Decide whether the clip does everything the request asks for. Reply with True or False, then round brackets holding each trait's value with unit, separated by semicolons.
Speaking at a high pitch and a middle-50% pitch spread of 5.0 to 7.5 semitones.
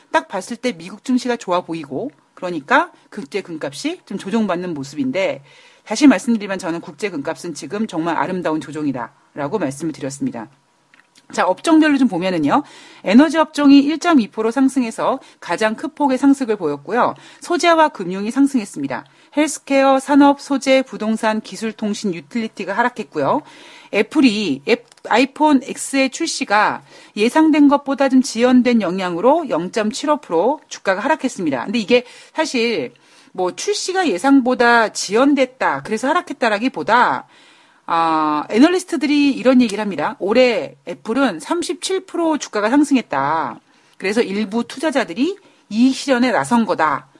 True (255 Hz; 5.6 semitones)